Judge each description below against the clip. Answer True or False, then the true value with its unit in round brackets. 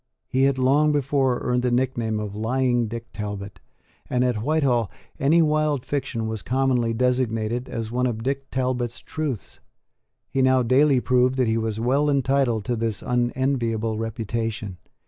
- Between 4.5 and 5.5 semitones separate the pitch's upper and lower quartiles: False (2.9 semitones)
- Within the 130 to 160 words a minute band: True (155 wpm)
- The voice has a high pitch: False (125 Hz)